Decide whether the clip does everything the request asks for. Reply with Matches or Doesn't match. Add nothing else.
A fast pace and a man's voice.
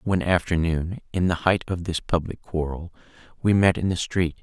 Doesn't match